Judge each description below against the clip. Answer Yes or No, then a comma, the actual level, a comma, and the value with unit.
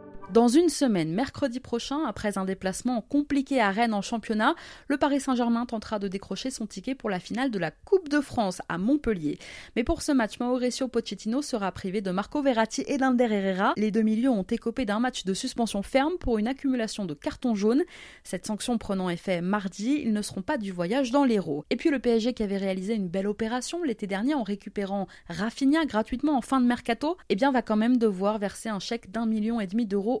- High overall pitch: Yes, high, 230 Hz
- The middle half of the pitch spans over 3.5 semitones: Yes, average, 4.6 semitones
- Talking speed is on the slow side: No, average, 215 wpm